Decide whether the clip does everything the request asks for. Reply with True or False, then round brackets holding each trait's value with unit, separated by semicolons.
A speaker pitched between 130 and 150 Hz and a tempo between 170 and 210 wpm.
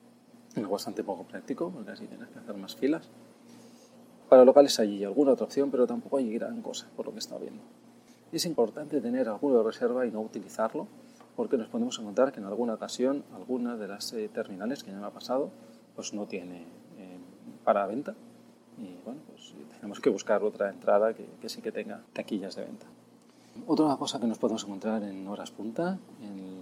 True (140 Hz; 185 wpm)